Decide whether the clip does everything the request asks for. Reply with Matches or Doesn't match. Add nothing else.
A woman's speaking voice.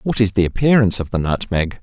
Doesn't match